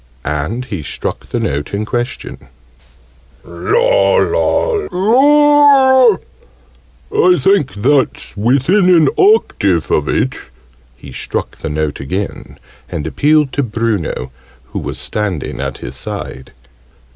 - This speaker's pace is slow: Yes, slow, 115 wpm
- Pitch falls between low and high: No, low, 125 Hz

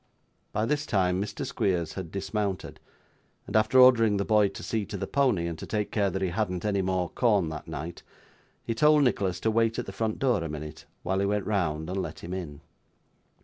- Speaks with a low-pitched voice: Yes, low, 100 Hz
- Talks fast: Yes, fast, 215 wpm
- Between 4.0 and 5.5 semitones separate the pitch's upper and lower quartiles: No, average, 3.5 semitones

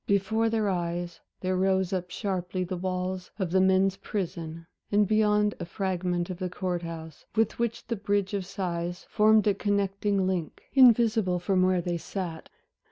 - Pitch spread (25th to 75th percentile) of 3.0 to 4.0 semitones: No, narrow, 2.4 semitones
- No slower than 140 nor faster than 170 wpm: Yes, average, 165 wpm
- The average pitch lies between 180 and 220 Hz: Yes, high, 190 Hz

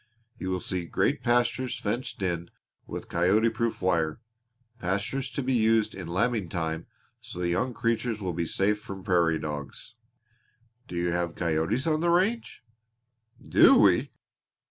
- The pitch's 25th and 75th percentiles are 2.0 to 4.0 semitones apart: No, average, 5.3 semitones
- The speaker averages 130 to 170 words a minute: Yes, average, 150 wpm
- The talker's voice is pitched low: Yes, very low, 95 Hz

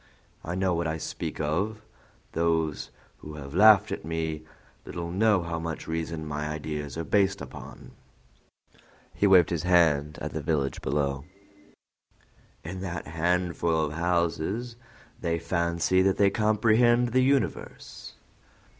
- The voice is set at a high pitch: No, very low, 85 Hz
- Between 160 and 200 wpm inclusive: No, slow, 135 wpm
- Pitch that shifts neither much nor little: Yes, average, 3.5 semitones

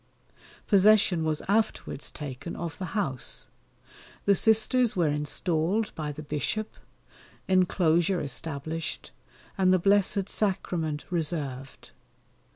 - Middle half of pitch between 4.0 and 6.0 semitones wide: Yes, average, 4.7 semitones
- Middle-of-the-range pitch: Yes, medium, 170 Hz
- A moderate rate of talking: No, slow, 100 wpm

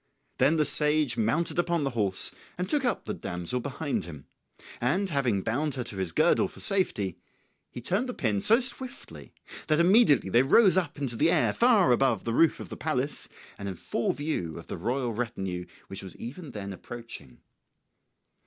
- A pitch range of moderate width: No, wide, 7.6 semitones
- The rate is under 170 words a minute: No, average, 185 wpm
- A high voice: No, low, 135 Hz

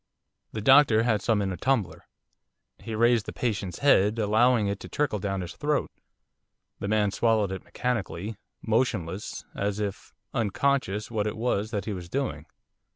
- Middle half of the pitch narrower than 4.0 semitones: Yes, average, 3.1 semitones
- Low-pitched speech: Yes, low, 110 Hz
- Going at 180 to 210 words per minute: No, average, 160 wpm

